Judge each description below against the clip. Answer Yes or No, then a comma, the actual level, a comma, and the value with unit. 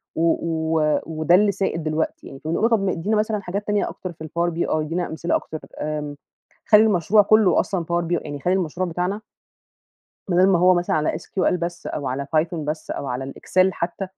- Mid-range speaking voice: Yes, medium, 170 Hz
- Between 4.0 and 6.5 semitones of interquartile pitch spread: No, average, 3.2 semitones